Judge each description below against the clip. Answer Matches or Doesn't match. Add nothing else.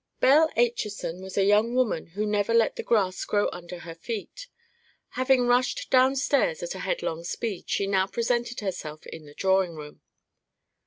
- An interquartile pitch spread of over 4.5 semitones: Matches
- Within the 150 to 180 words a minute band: Matches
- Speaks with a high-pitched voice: Matches